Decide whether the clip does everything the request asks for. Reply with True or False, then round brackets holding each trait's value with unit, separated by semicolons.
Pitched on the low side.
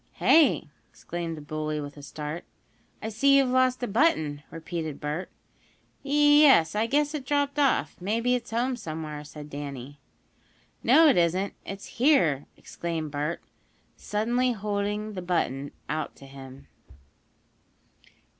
False (185 Hz)